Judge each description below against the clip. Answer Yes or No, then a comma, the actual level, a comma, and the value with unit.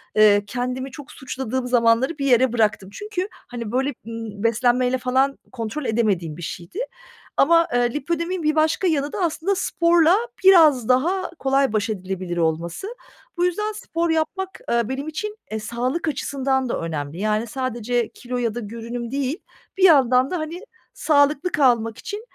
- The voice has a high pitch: Yes, very high, 255 Hz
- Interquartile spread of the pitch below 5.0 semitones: No, wide, 5.6 semitones